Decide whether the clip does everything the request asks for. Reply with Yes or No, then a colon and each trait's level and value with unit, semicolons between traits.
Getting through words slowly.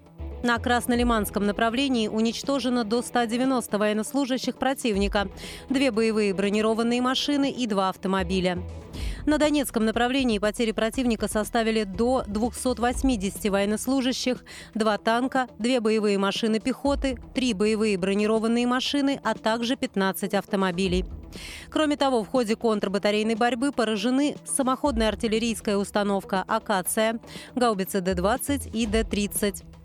Yes: slow, 105 wpm